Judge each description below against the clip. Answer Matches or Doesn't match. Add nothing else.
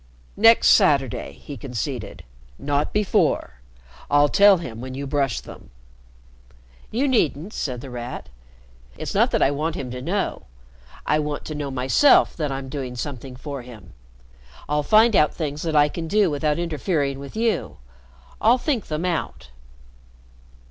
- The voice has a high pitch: Doesn't match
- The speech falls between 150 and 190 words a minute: Matches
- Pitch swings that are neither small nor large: Matches